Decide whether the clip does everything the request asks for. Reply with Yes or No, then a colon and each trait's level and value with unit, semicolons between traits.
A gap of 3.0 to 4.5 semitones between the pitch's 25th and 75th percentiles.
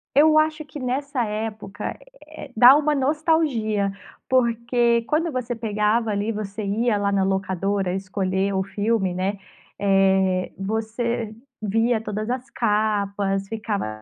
Yes: average, 3.6 semitones